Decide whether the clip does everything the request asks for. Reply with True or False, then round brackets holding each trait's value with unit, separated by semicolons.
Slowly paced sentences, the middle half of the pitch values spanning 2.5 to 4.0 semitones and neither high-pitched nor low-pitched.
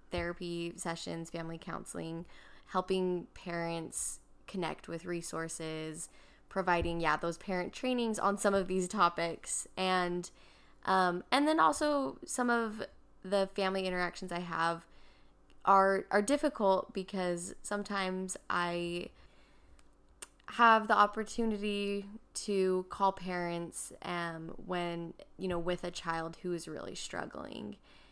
True (115 wpm; 2.8 semitones; 180 Hz)